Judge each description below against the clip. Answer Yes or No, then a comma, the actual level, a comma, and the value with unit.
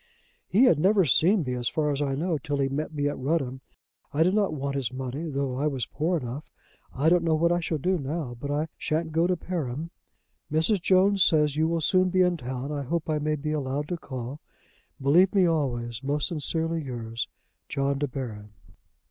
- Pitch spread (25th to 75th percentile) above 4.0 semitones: No, average, 3.7 semitones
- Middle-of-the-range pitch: Yes, medium, 150 Hz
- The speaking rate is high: Yes, fast, 210 wpm